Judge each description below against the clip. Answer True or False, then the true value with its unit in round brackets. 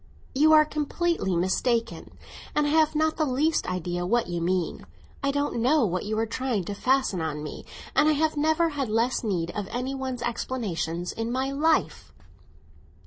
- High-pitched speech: True (250 Hz)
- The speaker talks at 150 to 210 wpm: True (180 wpm)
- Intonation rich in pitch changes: True (8.0 semitones)